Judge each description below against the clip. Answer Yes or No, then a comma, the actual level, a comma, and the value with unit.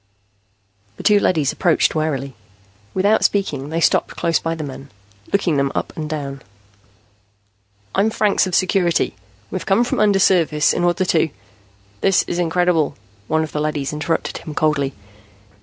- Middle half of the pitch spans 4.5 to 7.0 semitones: No, average, 4.0 semitones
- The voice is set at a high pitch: No, medium, 160 Hz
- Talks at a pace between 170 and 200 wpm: No, average, 155 wpm